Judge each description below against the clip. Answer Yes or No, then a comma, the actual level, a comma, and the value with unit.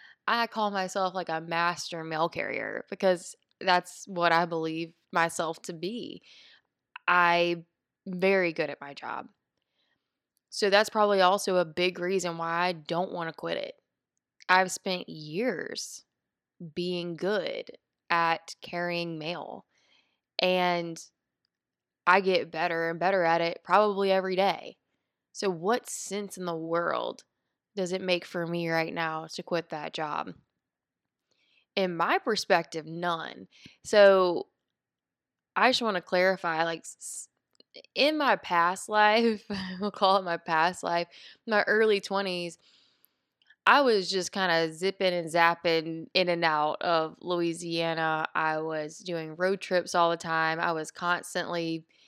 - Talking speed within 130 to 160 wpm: Yes, average, 140 wpm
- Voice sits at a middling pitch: Yes, medium, 175 Hz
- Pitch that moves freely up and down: No, narrow, 2.4 semitones